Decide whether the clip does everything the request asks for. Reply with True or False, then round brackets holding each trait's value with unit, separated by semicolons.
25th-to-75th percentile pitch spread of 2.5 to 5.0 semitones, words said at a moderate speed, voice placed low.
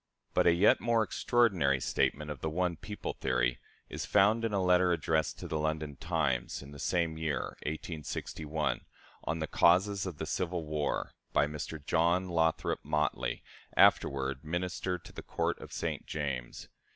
True (3.3 semitones; 165 wpm; 80 Hz)